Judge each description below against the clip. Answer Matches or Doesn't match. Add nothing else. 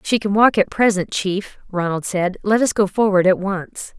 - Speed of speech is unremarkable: Doesn't match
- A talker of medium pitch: Doesn't match